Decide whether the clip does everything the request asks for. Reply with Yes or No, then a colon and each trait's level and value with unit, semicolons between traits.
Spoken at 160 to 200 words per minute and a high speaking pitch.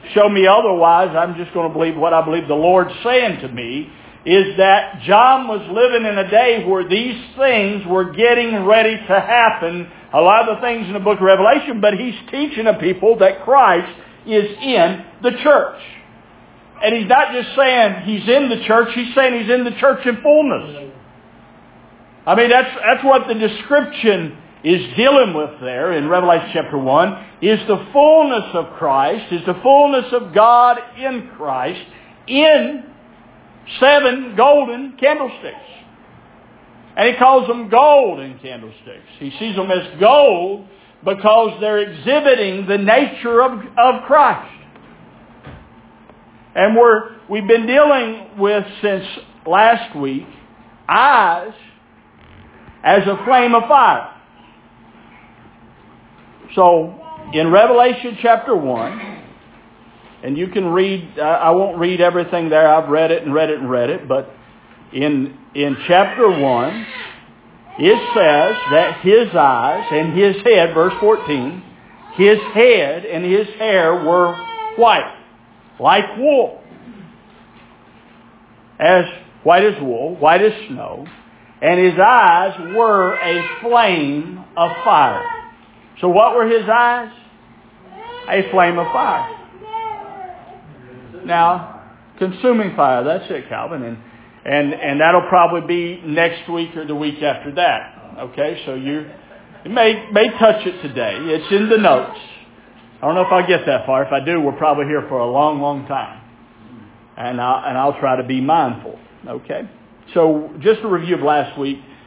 No: average, 145 wpm; high, 200 Hz